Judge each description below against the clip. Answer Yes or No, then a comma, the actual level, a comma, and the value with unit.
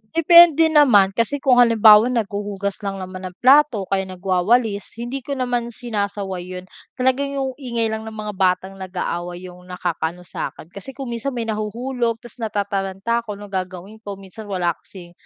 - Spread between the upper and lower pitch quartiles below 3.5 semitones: No, average, 4.2 semitones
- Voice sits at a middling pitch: No, high, 210 Hz